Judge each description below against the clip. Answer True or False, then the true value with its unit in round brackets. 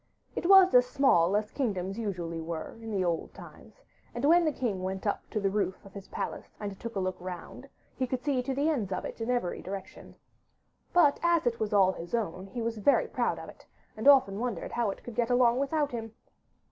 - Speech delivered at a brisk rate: True (225 wpm)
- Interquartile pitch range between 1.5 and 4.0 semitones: False (5.3 semitones)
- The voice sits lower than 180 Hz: False (225 Hz)